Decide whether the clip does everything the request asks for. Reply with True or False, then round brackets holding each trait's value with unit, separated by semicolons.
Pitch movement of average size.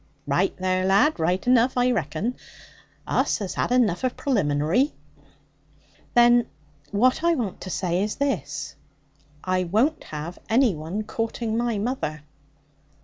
False (5.9 semitones)